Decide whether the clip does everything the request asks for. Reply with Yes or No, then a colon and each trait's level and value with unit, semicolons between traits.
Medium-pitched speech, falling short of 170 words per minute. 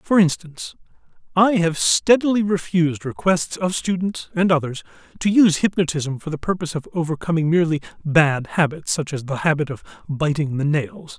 Yes: medium, 165 Hz; average, 160 wpm